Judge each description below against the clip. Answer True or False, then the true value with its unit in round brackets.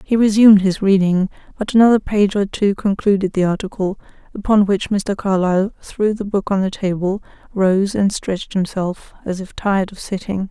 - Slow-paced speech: False (175 wpm)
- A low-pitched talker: False (195 Hz)